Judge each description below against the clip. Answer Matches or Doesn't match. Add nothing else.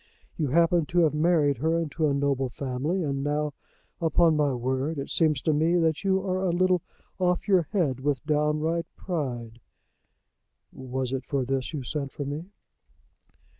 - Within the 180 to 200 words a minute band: Doesn't match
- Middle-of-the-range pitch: Matches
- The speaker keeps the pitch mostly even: Doesn't match